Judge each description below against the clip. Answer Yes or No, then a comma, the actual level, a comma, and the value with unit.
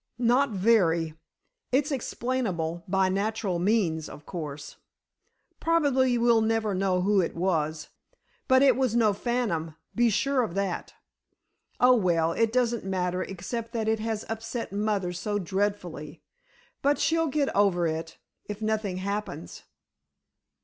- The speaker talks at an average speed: No, slow, 130 wpm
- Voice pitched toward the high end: Yes, high, 205 Hz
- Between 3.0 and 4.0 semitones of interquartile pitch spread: No, average, 4.9 semitones